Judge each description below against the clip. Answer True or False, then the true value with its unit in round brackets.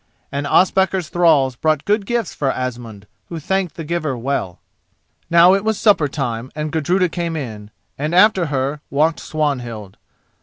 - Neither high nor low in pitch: True (155 Hz)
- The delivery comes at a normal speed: True (155 wpm)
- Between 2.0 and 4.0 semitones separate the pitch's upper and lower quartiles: False (5.0 semitones)